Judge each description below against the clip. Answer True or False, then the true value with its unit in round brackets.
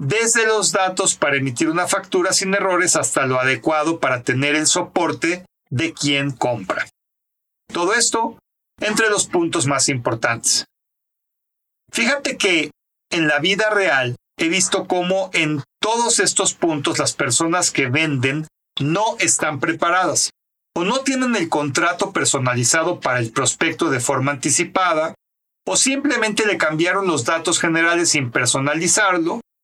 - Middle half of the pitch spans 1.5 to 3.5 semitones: False (5.2 semitones)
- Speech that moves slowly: False (135 wpm)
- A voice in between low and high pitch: True (165 Hz)